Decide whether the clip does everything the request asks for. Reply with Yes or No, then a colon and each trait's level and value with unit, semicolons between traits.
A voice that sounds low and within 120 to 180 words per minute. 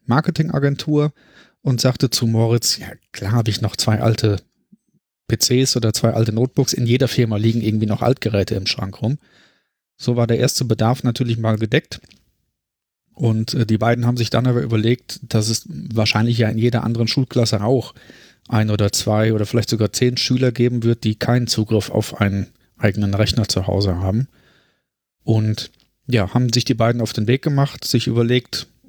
Yes: low, 115 Hz; average, 175 wpm